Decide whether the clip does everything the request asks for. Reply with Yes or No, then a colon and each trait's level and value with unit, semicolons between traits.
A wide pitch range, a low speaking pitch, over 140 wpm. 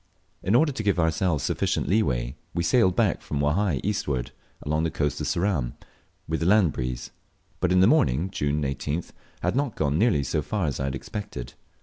Yes: wide, 6.1 semitones; very low, 80 Hz; average, 190 wpm